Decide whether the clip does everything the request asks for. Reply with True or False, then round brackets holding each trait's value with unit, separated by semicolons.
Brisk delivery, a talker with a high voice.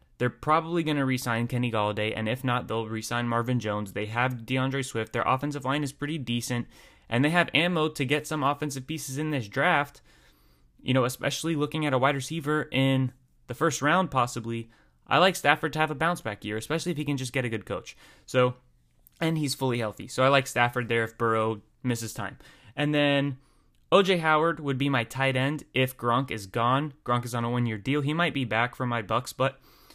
False (220 wpm; 130 Hz)